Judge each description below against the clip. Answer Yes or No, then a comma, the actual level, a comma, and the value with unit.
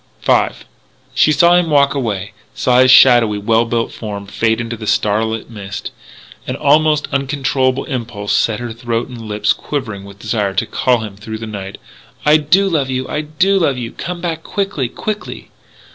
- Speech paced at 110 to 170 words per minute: No, average, 180 wpm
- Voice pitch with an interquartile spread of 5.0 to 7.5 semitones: Yes, average, 5.3 semitones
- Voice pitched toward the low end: Yes, low, 120 Hz